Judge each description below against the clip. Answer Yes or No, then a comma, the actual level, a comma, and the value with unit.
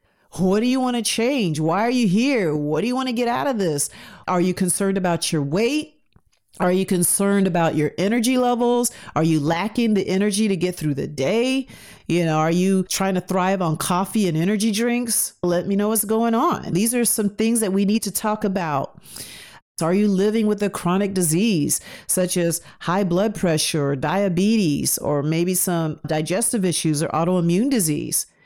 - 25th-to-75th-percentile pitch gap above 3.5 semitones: Yes, average, 4.8 semitones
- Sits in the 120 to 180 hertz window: No, high, 190 Hz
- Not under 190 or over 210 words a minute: Yes, average, 195 wpm